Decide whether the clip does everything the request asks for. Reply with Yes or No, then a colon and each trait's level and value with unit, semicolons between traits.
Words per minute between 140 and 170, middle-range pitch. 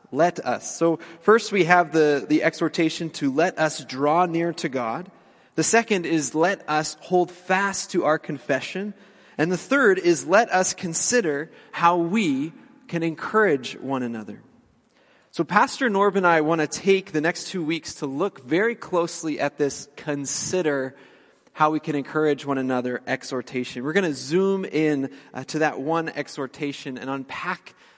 Yes: average, 165 wpm; medium, 160 Hz